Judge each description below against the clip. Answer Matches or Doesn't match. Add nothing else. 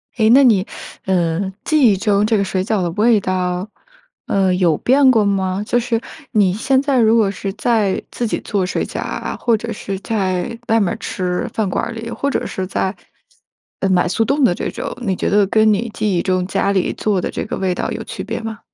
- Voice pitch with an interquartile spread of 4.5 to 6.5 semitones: Doesn't match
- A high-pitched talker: Matches